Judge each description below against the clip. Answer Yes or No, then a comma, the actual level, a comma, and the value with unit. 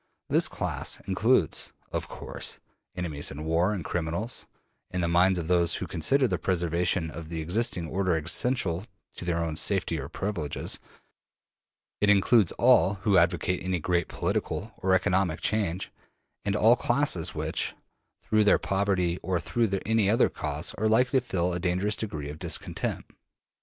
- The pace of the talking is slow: No, average, 155 wpm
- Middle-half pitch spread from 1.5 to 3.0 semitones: No, average, 3.5 semitones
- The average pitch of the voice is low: Yes, very low, 90 Hz